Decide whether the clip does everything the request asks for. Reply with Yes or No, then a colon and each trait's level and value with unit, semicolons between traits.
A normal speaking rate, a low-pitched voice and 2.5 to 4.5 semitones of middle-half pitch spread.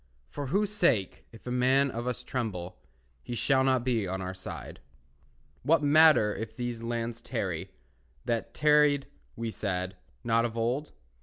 Yes: average, 155 wpm; low, 120 Hz; average, 3.6 semitones